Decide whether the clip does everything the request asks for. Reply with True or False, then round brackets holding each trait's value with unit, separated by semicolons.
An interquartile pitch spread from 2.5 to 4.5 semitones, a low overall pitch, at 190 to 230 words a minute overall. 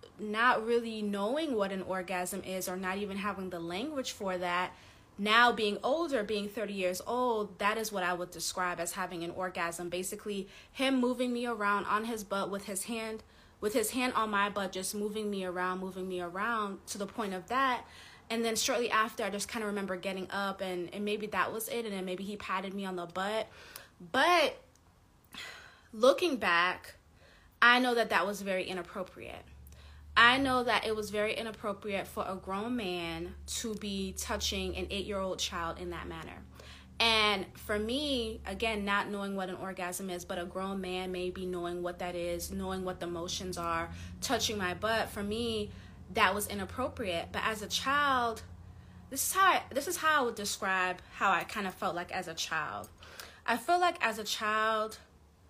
False (3.5 semitones; 200 Hz; 195 wpm)